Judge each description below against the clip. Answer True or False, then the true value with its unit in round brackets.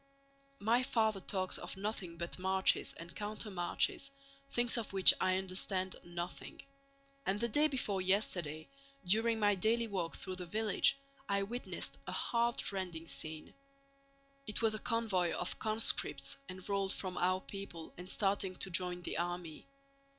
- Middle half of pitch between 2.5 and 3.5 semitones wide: True (3.2 semitones)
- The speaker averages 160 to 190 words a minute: False (145 wpm)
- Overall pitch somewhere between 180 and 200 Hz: True (190 Hz)